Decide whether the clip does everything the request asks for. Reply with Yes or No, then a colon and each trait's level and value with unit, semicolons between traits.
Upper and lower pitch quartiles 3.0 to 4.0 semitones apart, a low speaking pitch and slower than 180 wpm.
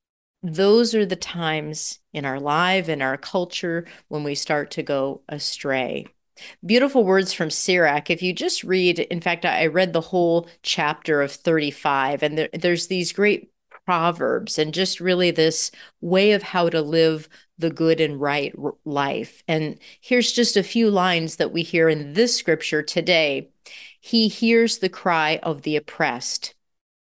No: average, 3.5 semitones; medium, 170 Hz; average, 160 wpm